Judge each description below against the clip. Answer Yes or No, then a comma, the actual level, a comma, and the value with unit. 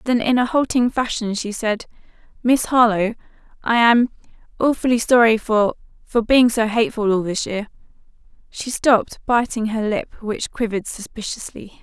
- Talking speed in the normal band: No, slow, 130 wpm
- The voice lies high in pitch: Yes, high, 225 Hz